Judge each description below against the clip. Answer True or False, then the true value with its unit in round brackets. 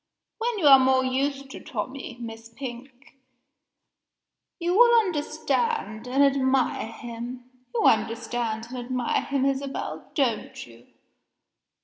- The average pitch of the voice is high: True (260 Hz)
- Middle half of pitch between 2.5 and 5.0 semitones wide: True (2.9 semitones)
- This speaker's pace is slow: True (115 wpm)